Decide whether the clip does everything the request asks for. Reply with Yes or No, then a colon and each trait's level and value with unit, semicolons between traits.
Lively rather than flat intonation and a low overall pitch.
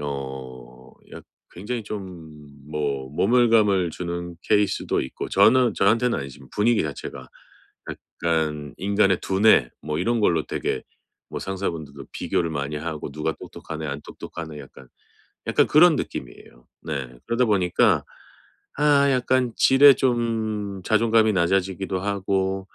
Yes: wide, 6.5 semitones; very low, 95 Hz